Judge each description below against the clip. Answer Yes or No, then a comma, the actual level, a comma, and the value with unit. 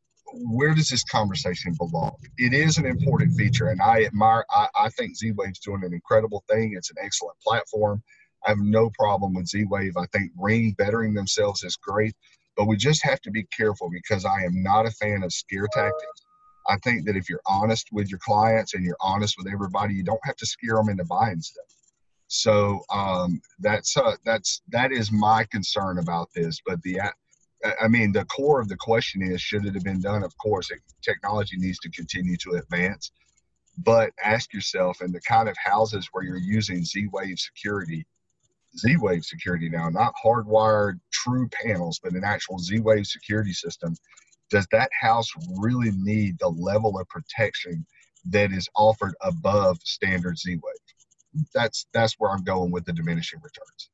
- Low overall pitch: Yes, low, 105 Hz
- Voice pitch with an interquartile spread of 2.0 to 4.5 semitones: Yes, average, 3.5 semitones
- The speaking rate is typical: Yes, average, 180 wpm